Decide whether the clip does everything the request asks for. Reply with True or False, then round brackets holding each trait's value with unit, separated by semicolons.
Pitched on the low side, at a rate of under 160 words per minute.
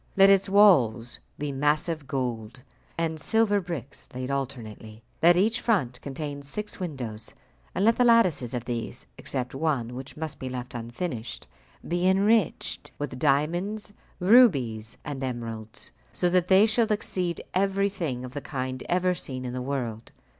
False (145 Hz; 150 wpm)